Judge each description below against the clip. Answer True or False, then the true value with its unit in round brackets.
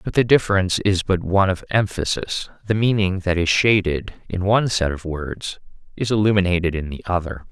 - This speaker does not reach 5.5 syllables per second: False (5.6 syllables/s)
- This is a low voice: True (95 Hz)